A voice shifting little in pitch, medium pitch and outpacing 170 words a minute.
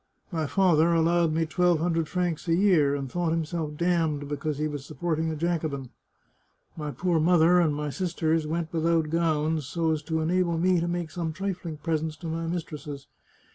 Yes: narrow, 1.9 semitones; medium, 165 Hz; average, 180 wpm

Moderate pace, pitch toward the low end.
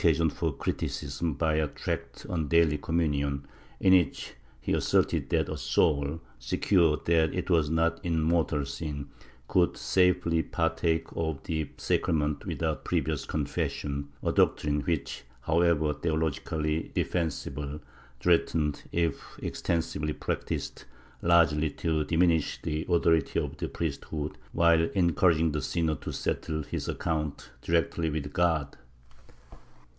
No: slow, 130 wpm; very low, 80 Hz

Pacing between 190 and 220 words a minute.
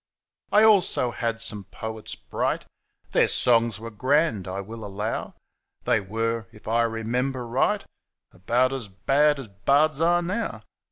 No: average, 155 wpm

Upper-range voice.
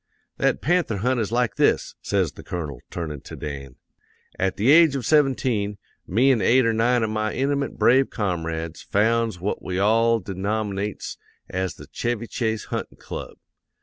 No: low, 110 Hz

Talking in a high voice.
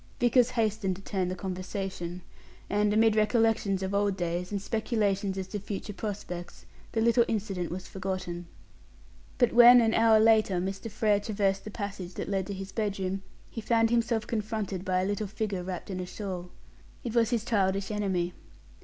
Yes: high, 200 Hz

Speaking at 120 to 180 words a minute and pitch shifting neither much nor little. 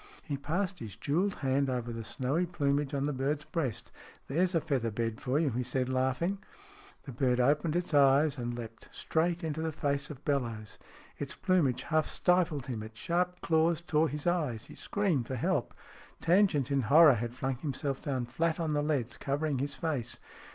No: average, 190 wpm; average, 4.2 semitones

